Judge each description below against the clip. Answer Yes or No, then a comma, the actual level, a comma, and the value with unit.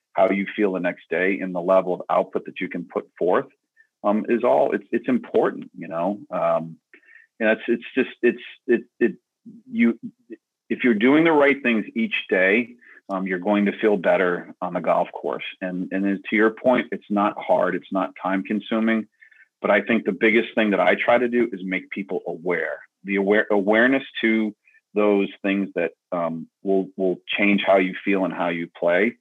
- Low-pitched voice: Yes, low, 105 Hz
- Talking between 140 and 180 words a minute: No, average, 200 wpm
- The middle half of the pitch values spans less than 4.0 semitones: No, average, 4.3 semitones